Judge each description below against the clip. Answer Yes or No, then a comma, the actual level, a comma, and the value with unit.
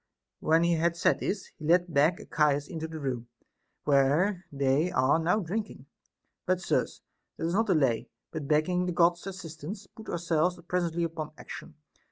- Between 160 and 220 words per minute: Yes, average, 165 wpm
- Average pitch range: Yes, average, 3.1 semitones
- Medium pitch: Yes, medium, 165 Hz